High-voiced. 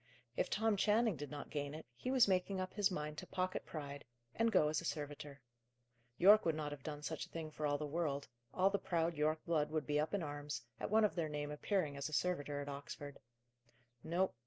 No: medium, 155 Hz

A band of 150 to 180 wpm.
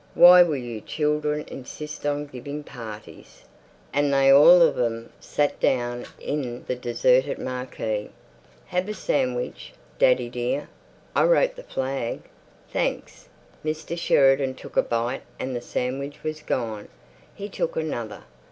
No: slow, 135 wpm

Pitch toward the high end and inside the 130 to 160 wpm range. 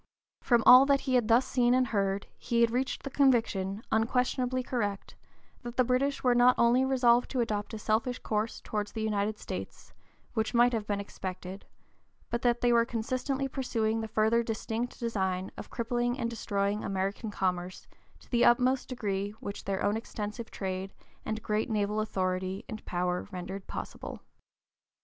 No: high, 225 Hz; average, 170 wpm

